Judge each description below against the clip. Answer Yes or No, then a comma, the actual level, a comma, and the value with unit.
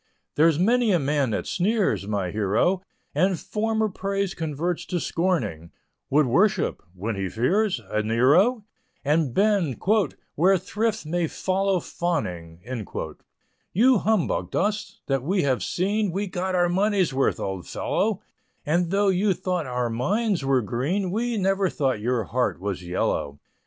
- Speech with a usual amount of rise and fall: No, wide, 7.8 semitones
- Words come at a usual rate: Yes, average, 145 wpm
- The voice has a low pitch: No, medium, 175 Hz